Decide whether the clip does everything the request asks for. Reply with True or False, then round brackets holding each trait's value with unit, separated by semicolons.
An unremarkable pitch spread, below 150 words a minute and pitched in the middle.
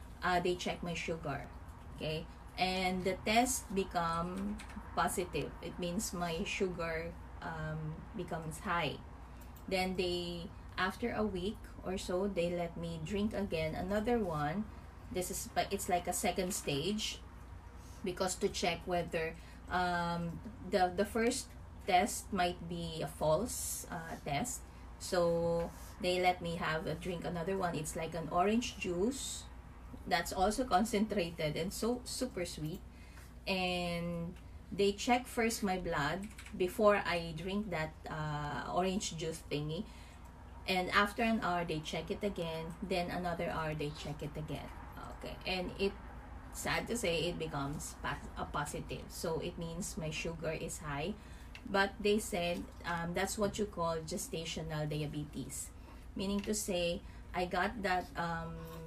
True (3.4 semitones; 140 wpm; 175 Hz)